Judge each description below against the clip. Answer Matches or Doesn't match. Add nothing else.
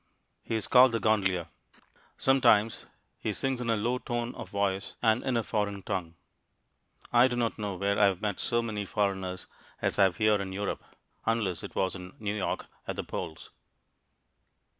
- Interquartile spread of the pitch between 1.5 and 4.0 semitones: Matches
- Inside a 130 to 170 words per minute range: Doesn't match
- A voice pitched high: Doesn't match